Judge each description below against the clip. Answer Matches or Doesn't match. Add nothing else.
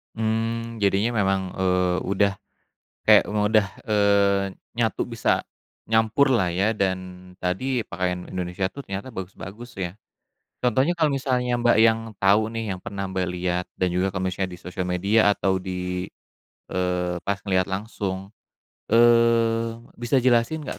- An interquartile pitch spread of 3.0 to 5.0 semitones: Matches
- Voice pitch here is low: Matches